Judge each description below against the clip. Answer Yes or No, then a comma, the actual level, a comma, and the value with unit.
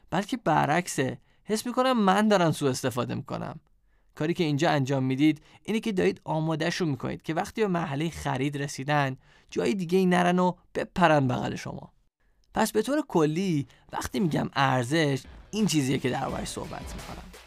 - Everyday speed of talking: No, fast, 160 wpm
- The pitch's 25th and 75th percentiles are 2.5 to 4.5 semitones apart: No, average, 5.1 semitones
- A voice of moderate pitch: Yes, medium, 160 Hz